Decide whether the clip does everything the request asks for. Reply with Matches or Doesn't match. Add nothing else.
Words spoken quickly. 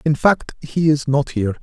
Matches